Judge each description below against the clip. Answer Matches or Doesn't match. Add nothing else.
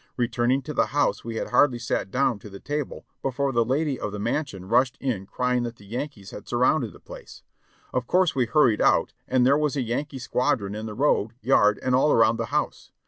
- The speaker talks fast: Matches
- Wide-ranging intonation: Doesn't match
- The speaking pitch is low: Matches